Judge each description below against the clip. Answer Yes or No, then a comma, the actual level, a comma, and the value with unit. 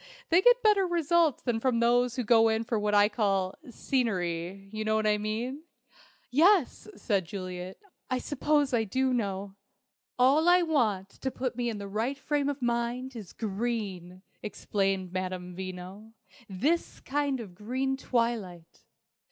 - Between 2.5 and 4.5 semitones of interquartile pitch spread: No, average, 5.2 semitones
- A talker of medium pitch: No, high, 230 Hz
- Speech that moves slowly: No, average, 155 wpm